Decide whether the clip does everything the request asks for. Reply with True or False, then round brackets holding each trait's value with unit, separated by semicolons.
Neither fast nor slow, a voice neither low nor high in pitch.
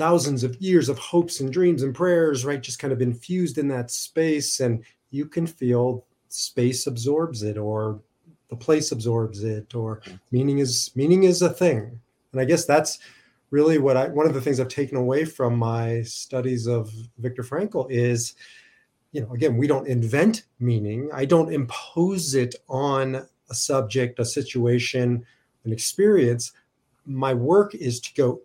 False (170 wpm; 130 Hz)